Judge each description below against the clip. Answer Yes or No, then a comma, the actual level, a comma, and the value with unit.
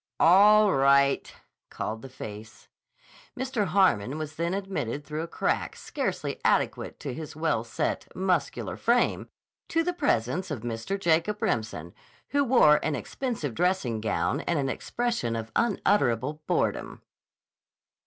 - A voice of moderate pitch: Yes, medium, 155 Hz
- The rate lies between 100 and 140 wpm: Yes, slow, 135 wpm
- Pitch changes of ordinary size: No, wide, 8.2 semitones